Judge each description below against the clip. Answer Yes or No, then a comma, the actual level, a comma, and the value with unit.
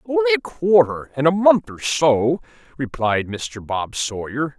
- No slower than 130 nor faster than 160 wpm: Yes, average, 155 wpm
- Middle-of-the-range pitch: Yes, medium, 155 Hz